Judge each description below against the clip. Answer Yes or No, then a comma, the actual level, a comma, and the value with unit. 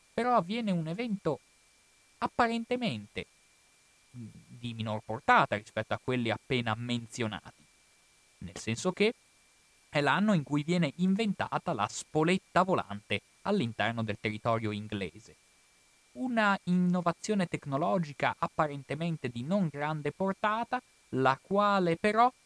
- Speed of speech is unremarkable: No, slow, 105 wpm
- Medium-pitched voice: Yes, medium, 160 Hz